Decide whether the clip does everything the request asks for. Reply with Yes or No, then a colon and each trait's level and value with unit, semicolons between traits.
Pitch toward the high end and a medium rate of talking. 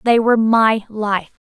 Yes: high, 215 Hz; average, 160 wpm